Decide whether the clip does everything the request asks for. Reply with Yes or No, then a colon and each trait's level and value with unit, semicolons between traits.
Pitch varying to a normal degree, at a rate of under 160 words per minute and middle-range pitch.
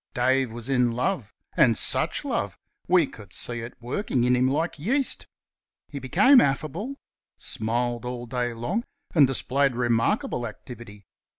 No: average, 3.7 semitones; average, 140 wpm; low, 125 Hz